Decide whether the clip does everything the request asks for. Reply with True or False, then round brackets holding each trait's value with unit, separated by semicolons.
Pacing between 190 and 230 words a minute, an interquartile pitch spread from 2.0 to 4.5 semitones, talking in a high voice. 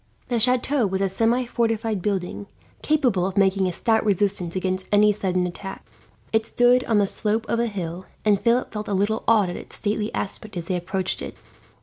True (200 wpm; 3.2 semitones; 205 Hz)